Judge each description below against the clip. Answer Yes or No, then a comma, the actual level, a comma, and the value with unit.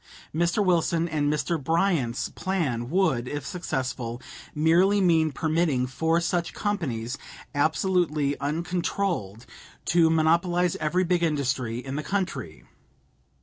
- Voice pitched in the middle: Yes, medium, 160 Hz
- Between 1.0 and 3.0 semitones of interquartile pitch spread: No, average, 4.2 semitones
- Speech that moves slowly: Yes, slow, 110 wpm